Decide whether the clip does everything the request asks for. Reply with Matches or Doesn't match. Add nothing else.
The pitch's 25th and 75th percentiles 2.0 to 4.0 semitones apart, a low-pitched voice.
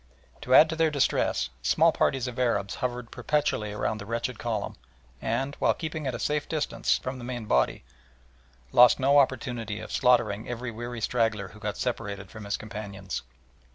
Matches